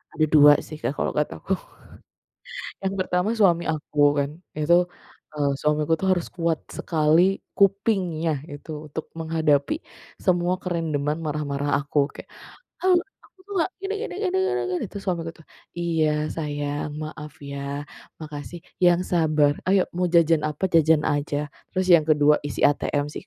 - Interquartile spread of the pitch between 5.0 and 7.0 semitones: No, average, 3.2 semitones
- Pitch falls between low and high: Yes, medium, 160 Hz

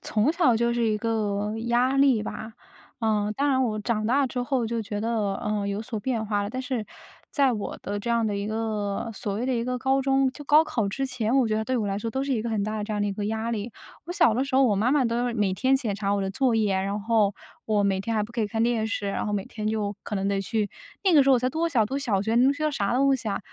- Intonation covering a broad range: No, average, 3.7 semitones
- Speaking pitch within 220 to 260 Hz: Yes, high, 225 Hz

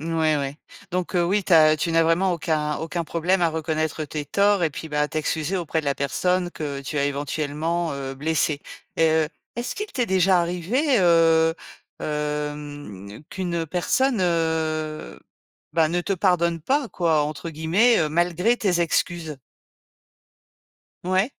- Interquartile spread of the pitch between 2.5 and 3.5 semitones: Yes, average, 2.8 semitones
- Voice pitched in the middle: Yes, medium, 165 Hz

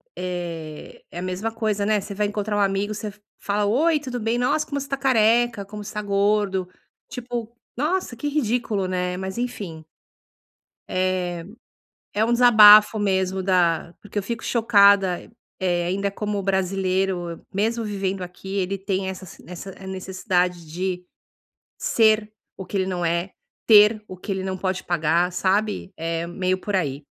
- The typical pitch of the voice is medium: No, high, 195 Hz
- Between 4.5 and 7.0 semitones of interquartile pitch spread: No, average, 2.8 semitones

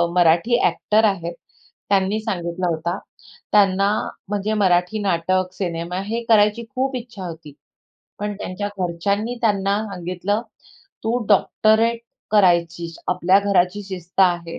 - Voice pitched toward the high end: Yes, high, 195 Hz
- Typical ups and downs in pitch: Yes, average, 3.2 semitones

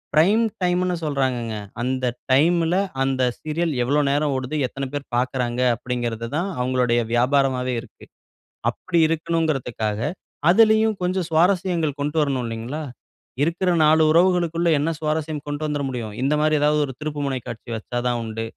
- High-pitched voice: No, medium, 145 Hz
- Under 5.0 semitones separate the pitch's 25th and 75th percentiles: Yes, average, 4.6 semitones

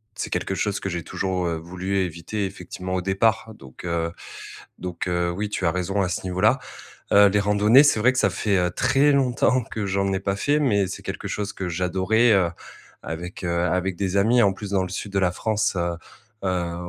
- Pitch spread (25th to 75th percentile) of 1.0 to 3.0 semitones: Yes, average, 2.7 semitones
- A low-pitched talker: Yes, very low, 95 Hz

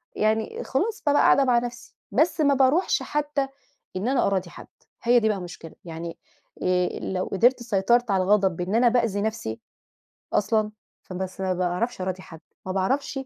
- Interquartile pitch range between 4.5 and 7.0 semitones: Yes, average, 5.0 semitones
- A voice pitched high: Yes, high, 215 Hz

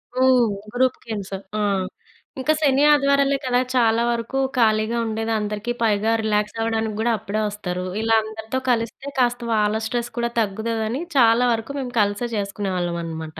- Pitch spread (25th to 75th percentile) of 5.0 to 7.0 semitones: No, average, 2.7 semitones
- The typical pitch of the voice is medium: No, high, 225 Hz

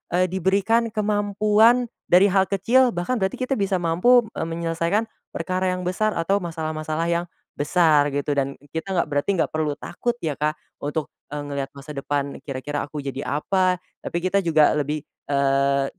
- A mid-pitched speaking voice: Yes, medium, 170 Hz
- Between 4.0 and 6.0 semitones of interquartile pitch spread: Yes, average, 5.0 semitones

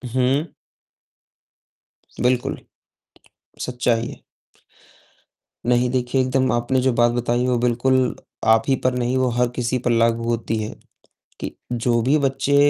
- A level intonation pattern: Yes, narrow, 1.5 semitones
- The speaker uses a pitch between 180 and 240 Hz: No, low, 125 Hz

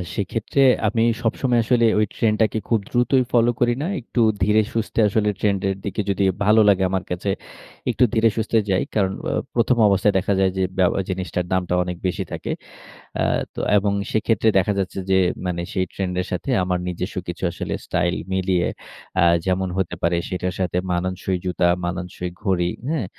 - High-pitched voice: No, very low, 95 Hz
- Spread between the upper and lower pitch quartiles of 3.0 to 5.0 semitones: Yes, average, 3.5 semitones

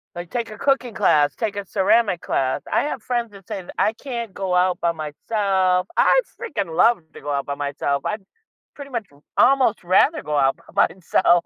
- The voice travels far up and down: Yes, wide, 5.7 semitones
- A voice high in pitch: Yes, high, 195 Hz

